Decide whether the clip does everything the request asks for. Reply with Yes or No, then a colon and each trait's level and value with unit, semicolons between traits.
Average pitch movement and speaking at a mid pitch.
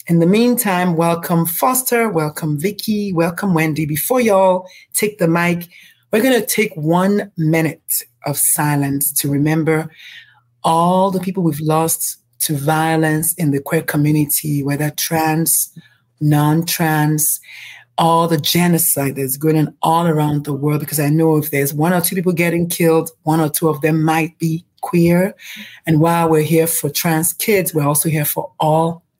No: narrow, 2.2 semitones; medium, 160 Hz